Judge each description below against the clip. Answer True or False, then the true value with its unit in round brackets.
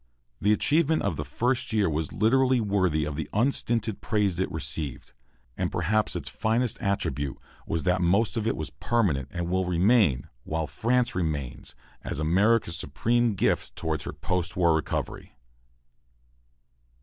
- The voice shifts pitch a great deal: True (6.1 semitones)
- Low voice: True (95 Hz)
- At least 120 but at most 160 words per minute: True (150 wpm)